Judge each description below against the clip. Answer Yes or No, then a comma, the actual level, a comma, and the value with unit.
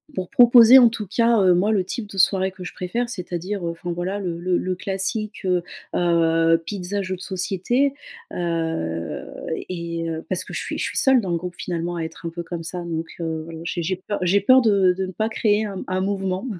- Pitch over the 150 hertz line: Yes, medium, 185 Hz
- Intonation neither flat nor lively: Yes, average, 3.1 semitones